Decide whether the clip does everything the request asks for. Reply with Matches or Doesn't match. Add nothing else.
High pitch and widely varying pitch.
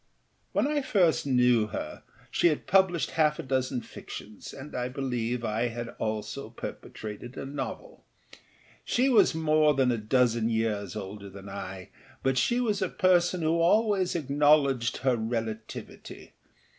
Doesn't match